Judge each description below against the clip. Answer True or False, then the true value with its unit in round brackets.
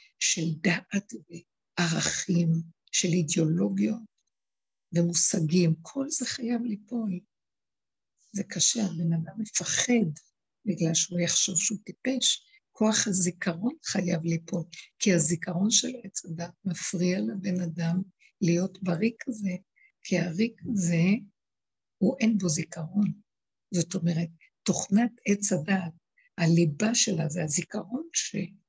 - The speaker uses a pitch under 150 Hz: False (185 Hz)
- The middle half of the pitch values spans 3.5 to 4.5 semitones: True (4.2 semitones)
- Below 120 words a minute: True (110 wpm)